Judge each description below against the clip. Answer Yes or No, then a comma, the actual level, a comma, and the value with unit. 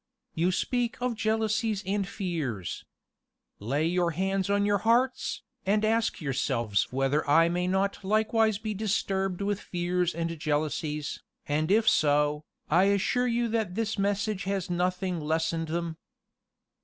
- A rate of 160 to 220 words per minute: No, average, 140 wpm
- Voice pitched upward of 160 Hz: Yes, medium, 185 Hz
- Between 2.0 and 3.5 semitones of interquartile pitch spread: No, average, 4.8 semitones